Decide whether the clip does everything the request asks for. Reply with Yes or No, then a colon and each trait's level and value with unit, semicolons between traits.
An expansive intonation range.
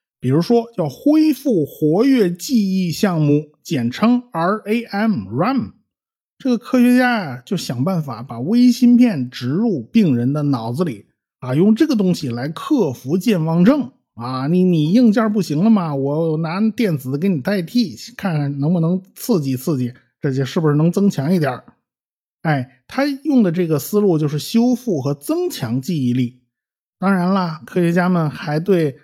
Yes: wide, 7.5 semitones